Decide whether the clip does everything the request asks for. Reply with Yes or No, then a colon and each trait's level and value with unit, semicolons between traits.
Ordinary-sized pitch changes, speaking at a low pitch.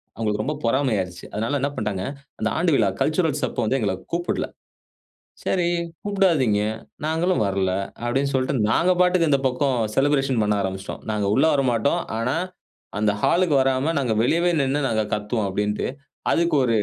No: wide, 6.3 semitones; low, 130 Hz